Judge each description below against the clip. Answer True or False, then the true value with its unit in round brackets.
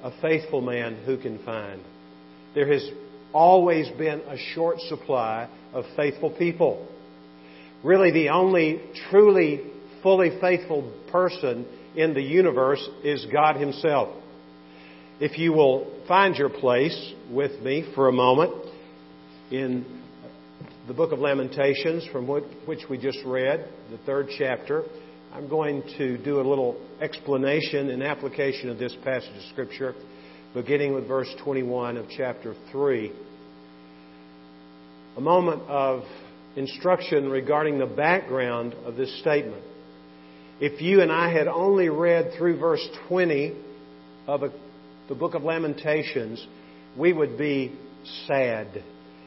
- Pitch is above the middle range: False (140 Hz)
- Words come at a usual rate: False (125 wpm)